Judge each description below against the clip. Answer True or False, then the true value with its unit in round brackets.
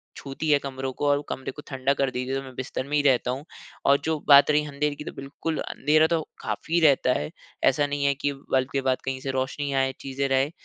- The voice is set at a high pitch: False (140 Hz)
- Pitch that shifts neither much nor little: False (1.7 semitones)